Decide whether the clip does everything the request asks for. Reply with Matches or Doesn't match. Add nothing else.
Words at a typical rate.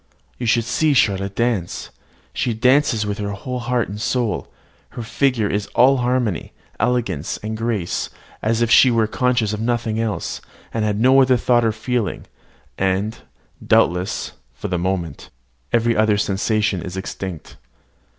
Matches